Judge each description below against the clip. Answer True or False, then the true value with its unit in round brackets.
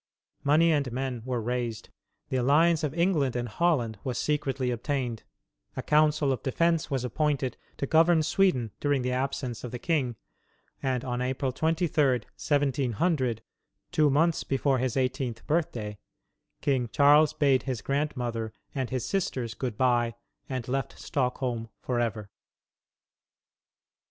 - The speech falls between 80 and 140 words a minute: True (135 wpm)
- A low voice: True (130 Hz)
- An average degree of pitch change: True (3.5 semitones)